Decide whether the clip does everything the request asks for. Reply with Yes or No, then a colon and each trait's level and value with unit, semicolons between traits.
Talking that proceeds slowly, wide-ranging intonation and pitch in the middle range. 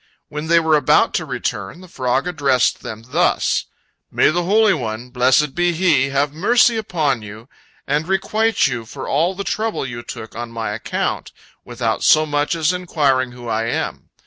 No: average, 175 wpm; wide, 6.2 semitones; medium, 145 Hz